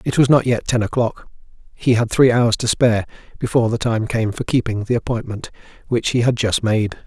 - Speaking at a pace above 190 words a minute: Yes, fast, 205 wpm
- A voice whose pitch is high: No, low, 115 Hz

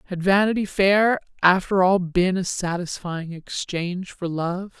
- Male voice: No, female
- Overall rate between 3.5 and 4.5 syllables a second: Yes, 4.2 syllables/s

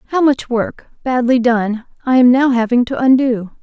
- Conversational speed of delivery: Yes, average, 180 wpm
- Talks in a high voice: Yes, high, 245 Hz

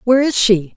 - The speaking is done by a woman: Yes, female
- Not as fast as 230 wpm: No, fast, 235 wpm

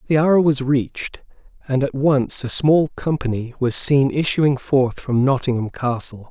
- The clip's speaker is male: Yes, male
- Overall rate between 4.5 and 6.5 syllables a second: No, 4.2 syllables/s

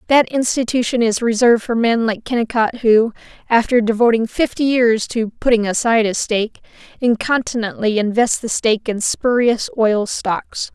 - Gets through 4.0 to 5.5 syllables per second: Yes, 5.0 syllables/s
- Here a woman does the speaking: Yes, female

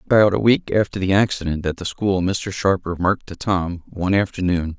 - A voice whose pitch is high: No, very low, 95 Hz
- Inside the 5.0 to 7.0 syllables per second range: Yes, 5.5 syllables/s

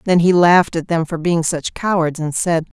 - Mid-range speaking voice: Yes, medium, 165 Hz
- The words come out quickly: Yes, fast, 235 wpm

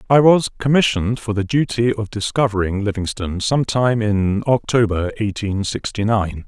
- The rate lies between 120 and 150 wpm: Yes, average, 140 wpm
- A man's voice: Yes, male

